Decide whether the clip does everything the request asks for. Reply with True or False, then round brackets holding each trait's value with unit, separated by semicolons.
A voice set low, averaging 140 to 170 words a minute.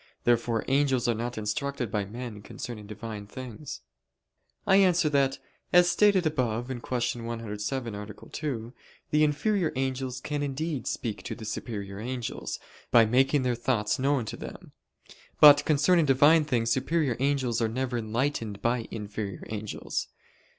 True (125 Hz; 145 wpm)